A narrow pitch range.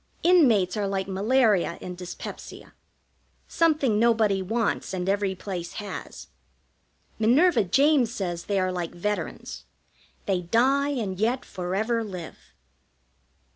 No: average, 4.4 semitones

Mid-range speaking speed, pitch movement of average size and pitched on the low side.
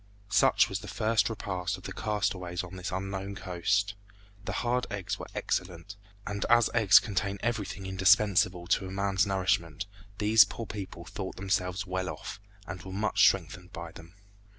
No: average, 160 wpm; narrow, 2.1 semitones; very low, 95 Hz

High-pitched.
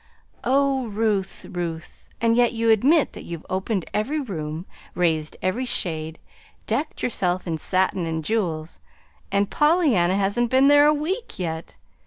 Yes: high, 200 Hz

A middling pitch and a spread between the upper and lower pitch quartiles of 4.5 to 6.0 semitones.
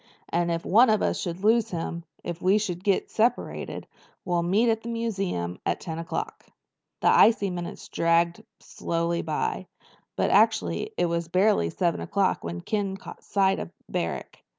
No: medium, 180 Hz; average, 3.9 semitones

